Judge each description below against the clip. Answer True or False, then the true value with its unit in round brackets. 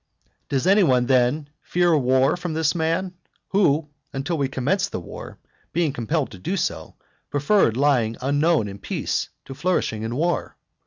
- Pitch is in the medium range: True (145 Hz)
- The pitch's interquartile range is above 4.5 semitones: True (5.2 semitones)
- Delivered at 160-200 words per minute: True (165 wpm)